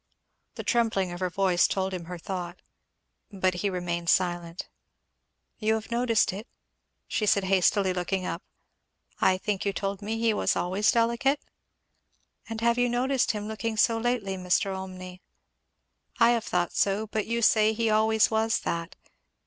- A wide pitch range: No, average, 3.5 semitones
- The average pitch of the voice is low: No, high, 200 Hz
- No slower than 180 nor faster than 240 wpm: No, average, 165 wpm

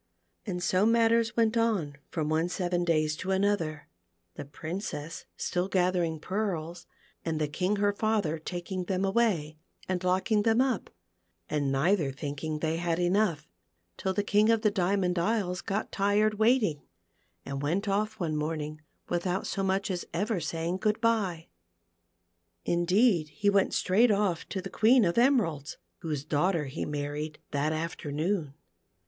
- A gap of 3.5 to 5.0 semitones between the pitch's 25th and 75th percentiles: Yes, average, 4.6 semitones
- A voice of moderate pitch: Yes, medium, 180 Hz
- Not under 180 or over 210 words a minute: No, average, 155 wpm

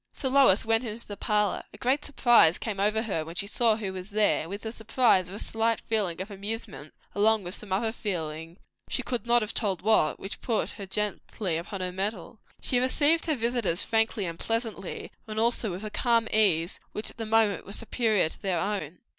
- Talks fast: Yes, fast, 210 wpm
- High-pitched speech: Yes, high, 210 Hz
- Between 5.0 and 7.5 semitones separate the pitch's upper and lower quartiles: No, average, 3.1 semitones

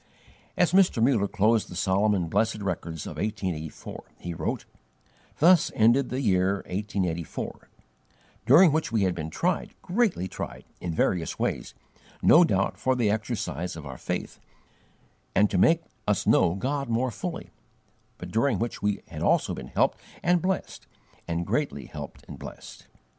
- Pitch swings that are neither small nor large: No, wide, 6.7 semitones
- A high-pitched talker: No, low, 105 Hz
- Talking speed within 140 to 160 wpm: Yes, average, 155 wpm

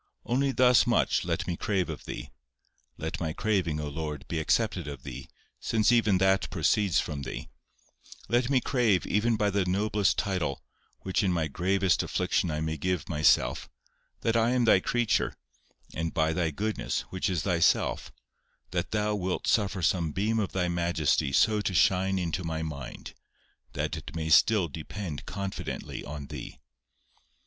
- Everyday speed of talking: Yes, average, 165 wpm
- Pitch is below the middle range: Yes, very low, 90 Hz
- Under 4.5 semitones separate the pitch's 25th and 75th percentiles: No, average, 4.8 semitones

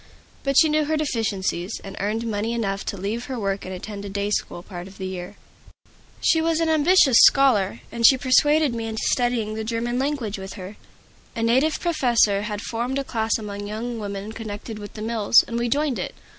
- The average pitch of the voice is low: No, high, 225 Hz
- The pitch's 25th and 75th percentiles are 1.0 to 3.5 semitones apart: No, average, 4.2 semitones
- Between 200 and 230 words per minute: Yes, fast, 205 wpm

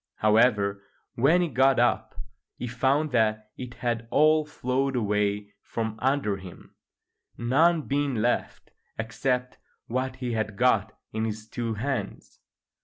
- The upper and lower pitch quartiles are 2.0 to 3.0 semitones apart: No, average, 3.6 semitones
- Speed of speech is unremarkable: No, slow, 130 wpm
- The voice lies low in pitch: Yes, low, 120 Hz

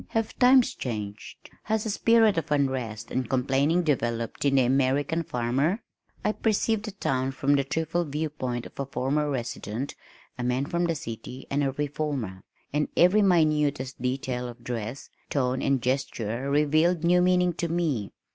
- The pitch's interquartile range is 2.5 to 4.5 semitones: No, average, 4.9 semitones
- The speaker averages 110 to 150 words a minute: No, average, 160 wpm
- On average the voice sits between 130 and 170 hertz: Yes, medium, 140 Hz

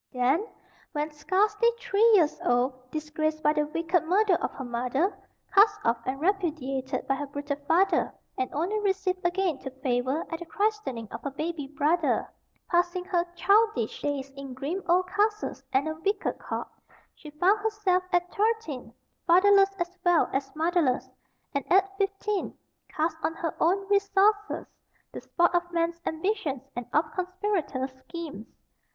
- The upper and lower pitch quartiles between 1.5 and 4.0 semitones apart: No, wide, 5.6 semitones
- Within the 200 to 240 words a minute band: No, average, 155 wpm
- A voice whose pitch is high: Yes, very high, 335 Hz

